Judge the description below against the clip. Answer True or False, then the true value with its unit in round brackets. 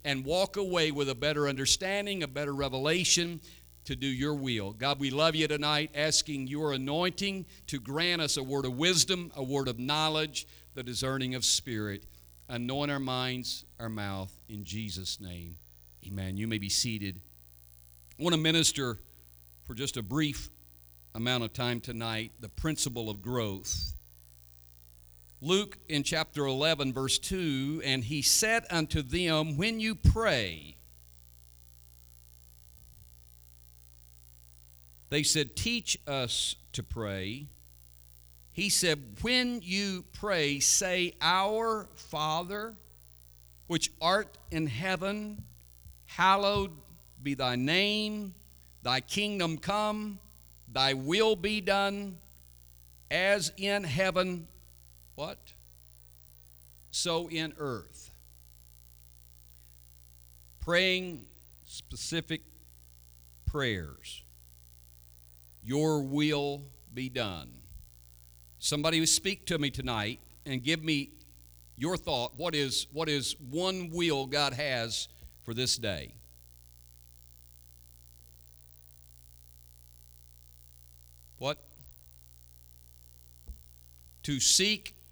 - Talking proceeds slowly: True (105 wpm)